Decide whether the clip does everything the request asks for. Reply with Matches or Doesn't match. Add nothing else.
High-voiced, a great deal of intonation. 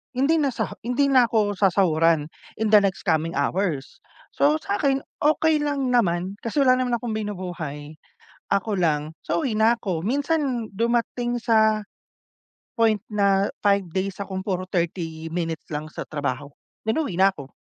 Matches